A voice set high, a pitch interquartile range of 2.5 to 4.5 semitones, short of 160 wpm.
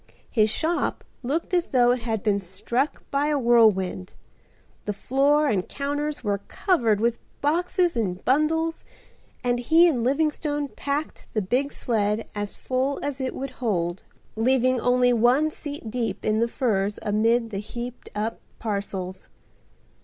No: high, 245 Hz; average, 5.1 semitones; average, 145 wpm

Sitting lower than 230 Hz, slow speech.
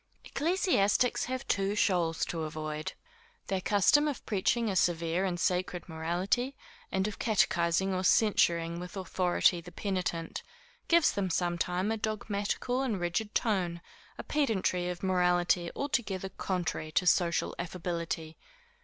Yes: medium, 185 Hz; slow, 130 wpm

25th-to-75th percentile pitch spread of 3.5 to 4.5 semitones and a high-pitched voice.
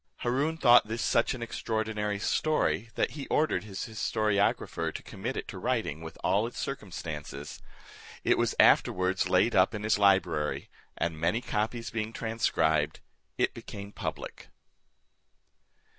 No: average, 3.9 semitones; low, 105 Hz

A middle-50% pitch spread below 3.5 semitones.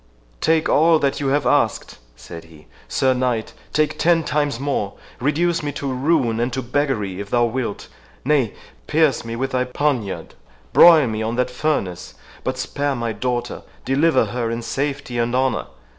No: average, 3.8 semitones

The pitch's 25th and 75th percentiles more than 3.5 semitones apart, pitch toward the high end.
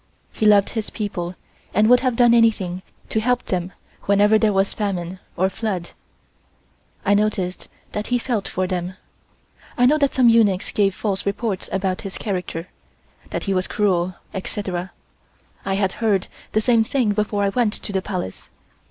No: average, 2.9 semitones; high, 200 Hz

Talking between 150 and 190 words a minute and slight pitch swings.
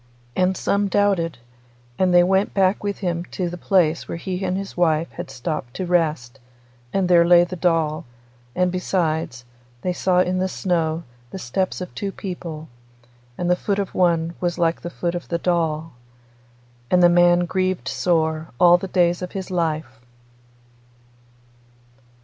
Yes: average, 165 wpm; narrow, 2.0 semitones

